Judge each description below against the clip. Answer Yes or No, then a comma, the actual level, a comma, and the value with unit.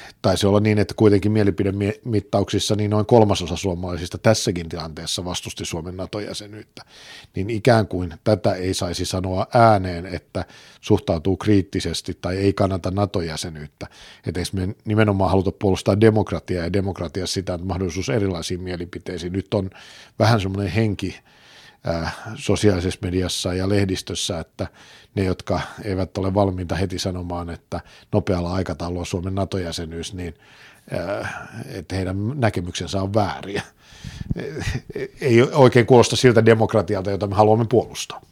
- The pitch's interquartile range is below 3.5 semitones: Yes, narrow, 2.6 semitones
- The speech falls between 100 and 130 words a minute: Yes, average, 125 wpm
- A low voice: Yes, very low, 95 Hz